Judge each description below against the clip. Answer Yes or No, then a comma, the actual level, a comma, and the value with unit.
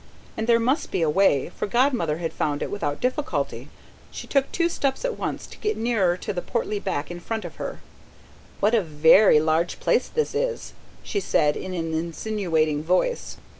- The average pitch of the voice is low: No, high, 195 Hz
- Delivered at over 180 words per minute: Yes, average, 190 wpm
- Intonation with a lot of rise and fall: Yes, wide, 7.3 semitones